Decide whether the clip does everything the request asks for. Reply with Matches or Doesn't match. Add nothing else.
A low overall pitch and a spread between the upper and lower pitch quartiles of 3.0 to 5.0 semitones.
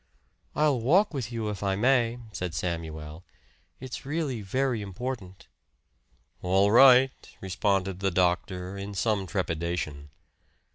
Doesn't match